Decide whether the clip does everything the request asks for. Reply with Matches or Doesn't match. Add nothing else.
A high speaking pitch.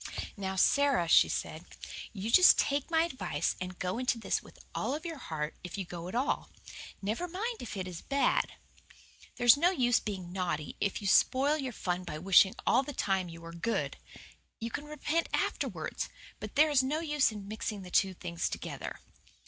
Matches